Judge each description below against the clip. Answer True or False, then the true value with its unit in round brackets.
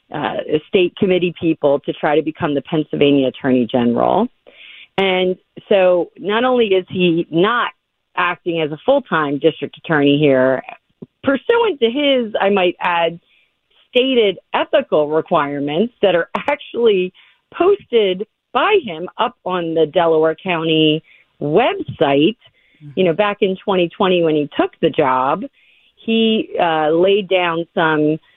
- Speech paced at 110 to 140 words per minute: True (135 wpm)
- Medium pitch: True (180 Hz)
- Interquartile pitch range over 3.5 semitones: True (5.2 semitones)